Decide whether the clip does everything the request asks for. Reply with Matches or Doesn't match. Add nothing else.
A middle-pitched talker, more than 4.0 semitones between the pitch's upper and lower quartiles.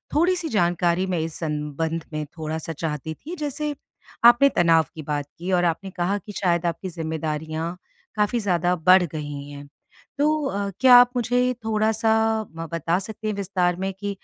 Matches